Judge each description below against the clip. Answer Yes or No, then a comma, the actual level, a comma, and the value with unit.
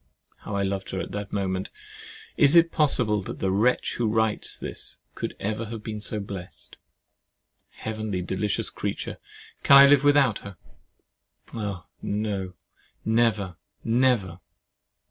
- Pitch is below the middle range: Yes, low, 105 Hz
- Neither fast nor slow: No, slow, 125 wpm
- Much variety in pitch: No, average, 3.0 semitones